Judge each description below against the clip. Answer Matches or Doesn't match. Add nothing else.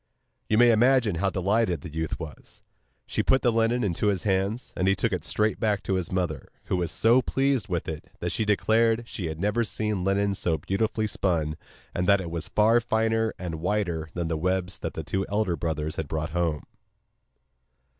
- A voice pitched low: Matches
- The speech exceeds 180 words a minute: Matches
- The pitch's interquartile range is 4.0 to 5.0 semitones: Matches